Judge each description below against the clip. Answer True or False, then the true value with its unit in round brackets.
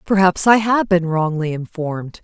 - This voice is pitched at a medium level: True (175 Hz)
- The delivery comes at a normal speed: True (160 wpm)